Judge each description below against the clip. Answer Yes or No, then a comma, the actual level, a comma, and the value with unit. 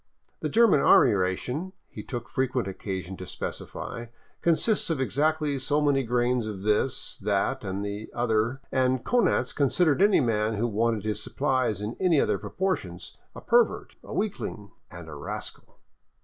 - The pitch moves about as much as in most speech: No, wide, 5.7 semitones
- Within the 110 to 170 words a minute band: Yes, average, 155 wpm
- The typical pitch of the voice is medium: No, low, 125 Hz